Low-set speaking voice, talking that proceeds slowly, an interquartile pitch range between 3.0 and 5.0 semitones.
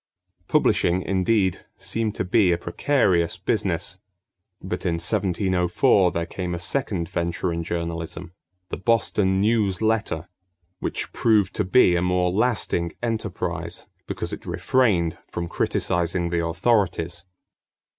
Yes: very low, 90 Hz; slow, 125 wpm; average, 3.6 semitones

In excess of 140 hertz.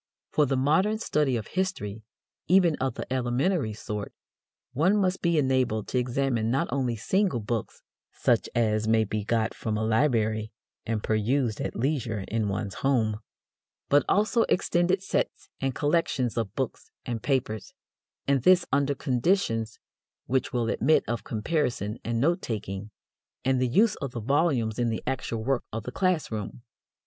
No: low, 125 Hz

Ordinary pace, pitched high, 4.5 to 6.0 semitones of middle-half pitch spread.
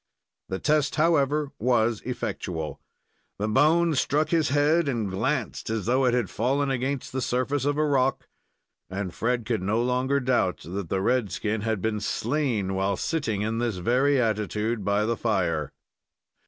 No: average, 165 wpm; low, 120 Hz; average, 5.0 semitones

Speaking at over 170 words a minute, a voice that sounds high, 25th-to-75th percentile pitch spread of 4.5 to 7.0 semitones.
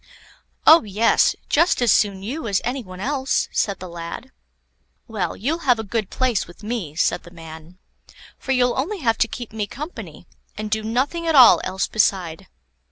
Yes: average, 180 wpm; high, 220 Hz; wide, 5.6 semitones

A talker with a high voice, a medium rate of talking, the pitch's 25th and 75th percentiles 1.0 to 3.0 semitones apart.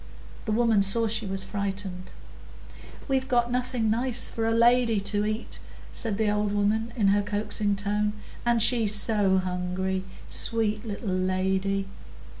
Yes: high, 210 Hz; average, 145 wpm; narrow, 2.6 semitones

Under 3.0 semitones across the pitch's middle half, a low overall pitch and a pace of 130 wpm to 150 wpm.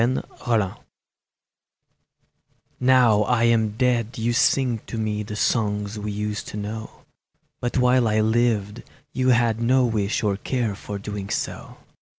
Yes: narrow, 2.5 semitones; low, 110 Hz; average, 145 wpm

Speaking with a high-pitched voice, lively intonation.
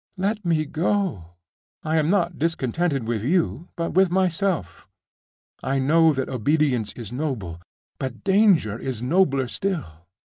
No: medium, 155 Hz; wide, 6.1 semitones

